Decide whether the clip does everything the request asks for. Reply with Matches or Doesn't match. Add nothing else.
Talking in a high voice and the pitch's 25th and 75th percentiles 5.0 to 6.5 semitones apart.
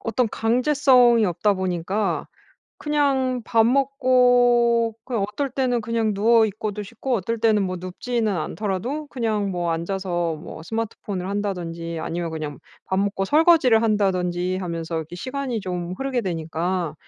Matches